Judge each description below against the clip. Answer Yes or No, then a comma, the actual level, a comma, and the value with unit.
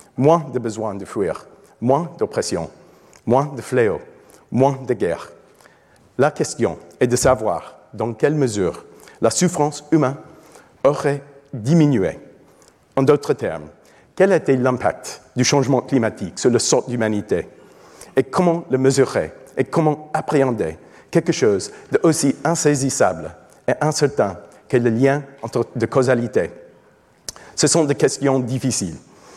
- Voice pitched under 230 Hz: Yes, low, 135 Hz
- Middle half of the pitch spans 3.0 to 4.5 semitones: Yes, average, 3.5 semitones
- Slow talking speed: Yes, slow, 125 wpm